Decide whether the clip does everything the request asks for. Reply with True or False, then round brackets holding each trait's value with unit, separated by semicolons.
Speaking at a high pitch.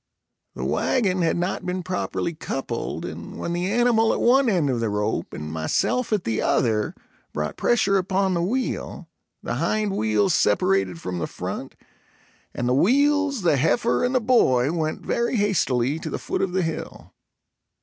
False (175 Hz)